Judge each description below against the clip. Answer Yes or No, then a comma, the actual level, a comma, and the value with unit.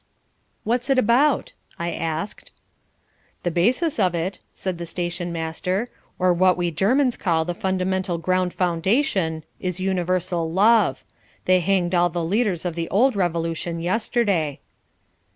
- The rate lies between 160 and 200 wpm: No, slow, 135 wpm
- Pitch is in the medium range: Yes, medium, 180 Hz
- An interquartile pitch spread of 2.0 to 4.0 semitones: Yes, average, 2.8 semitones